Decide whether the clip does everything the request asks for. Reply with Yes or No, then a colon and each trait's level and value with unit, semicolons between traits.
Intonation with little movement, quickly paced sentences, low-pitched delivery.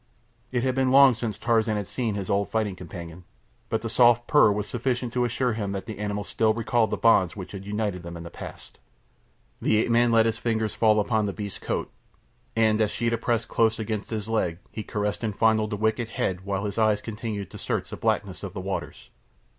Yes: narrow, 2.2 semitones; fast, 220 wpm; low, 110 Hz